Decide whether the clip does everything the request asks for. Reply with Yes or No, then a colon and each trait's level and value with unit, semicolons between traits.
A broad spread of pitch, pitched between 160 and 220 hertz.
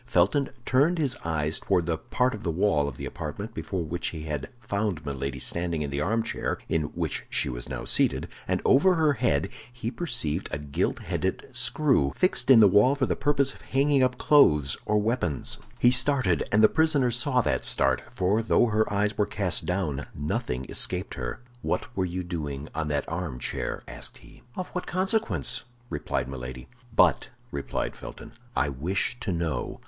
No: wide, 8.8 semitones; very low, 95 Hz